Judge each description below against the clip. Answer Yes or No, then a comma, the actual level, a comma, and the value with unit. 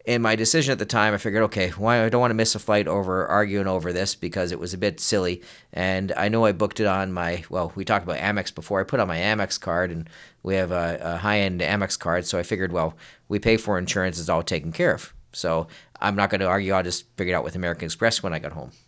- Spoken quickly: Yes, fast, 275 wpm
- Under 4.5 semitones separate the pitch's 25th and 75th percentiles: Yes, average, 3.0 semitones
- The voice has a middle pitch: No, very low, 95 Hz